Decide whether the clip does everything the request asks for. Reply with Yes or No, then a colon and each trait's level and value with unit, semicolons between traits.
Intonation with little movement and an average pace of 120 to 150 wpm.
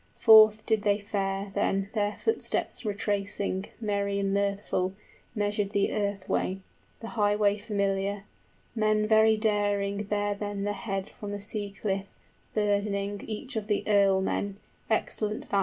Yes: narrow, 1.1 semitones; average, 140 wpm